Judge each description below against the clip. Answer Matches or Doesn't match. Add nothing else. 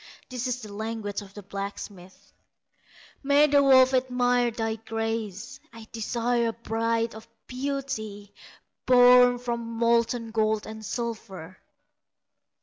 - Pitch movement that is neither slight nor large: Doesn't match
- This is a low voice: Doesn't match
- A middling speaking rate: Doesn't match